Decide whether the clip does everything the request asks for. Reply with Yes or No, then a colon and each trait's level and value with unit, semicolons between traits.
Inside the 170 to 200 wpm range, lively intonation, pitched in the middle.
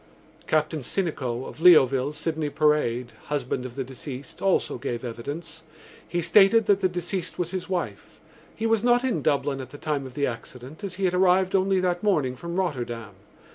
Yes: average, 180 wpm; wide, 5.9 semitones; medium, 155 Hz